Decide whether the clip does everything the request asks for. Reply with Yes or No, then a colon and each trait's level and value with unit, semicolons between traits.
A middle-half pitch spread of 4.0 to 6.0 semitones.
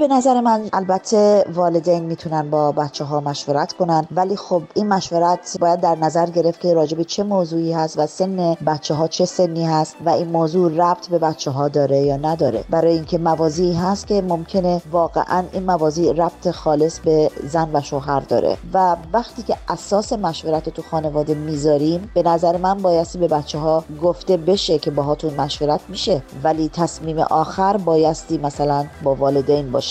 No: narrow, 2.6 semitones